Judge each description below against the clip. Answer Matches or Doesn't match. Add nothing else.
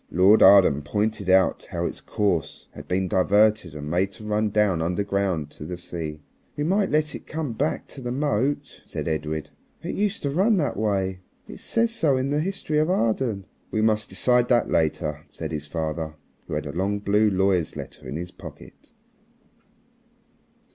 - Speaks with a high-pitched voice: Doesn't match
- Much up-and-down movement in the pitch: Matches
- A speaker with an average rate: Matches